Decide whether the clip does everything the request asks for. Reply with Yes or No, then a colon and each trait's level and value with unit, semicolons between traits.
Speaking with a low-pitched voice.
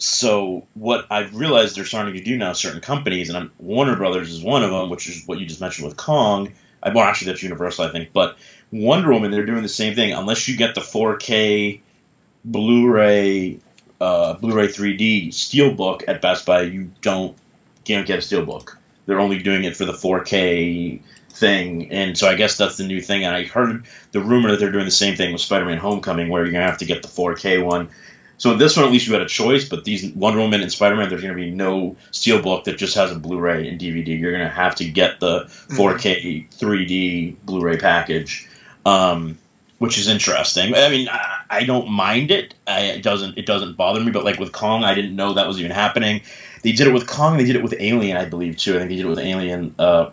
Yes: low, 100 Hz